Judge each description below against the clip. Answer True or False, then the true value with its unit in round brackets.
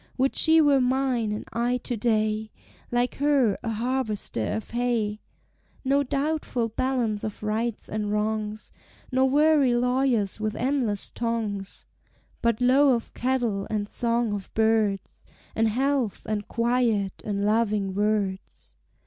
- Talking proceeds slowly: True (130 wpm)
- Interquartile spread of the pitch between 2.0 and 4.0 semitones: True (3.3 semitones)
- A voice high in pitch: True (230 Hz)